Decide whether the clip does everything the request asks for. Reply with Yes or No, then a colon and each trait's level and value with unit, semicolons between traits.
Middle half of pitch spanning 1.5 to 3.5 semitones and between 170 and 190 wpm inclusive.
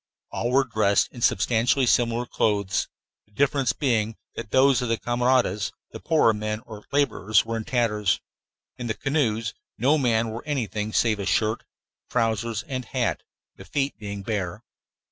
No: average, 2.9 semitones; average, 160 wpm